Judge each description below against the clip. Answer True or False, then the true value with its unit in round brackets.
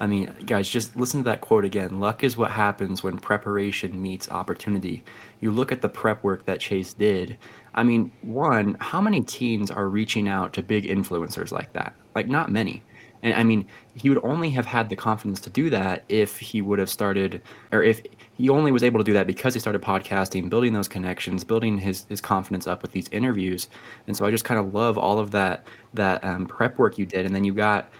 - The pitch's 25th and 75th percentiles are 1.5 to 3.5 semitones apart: True (3.0 semitones)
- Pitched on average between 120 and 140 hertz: False (105 Hz)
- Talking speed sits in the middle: False (225 wpm)